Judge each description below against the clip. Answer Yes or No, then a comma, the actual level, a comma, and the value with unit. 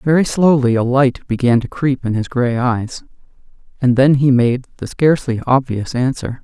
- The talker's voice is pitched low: Yes, low, 130 Hz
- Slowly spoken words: No, average, 175 wpm